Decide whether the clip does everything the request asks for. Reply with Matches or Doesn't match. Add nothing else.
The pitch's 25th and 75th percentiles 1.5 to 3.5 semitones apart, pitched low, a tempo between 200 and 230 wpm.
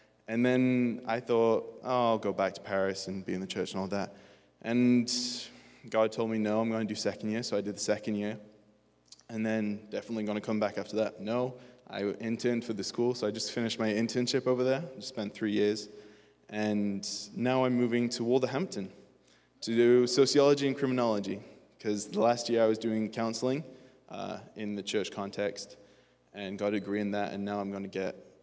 Matches